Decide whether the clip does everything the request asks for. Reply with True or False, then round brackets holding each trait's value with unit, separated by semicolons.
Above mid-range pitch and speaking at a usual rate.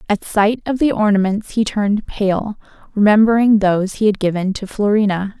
True (205 Hz; 165 wpm)